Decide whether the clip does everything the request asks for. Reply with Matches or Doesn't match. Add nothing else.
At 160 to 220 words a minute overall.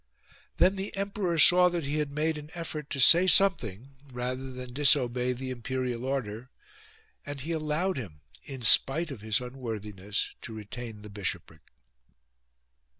Doesn't match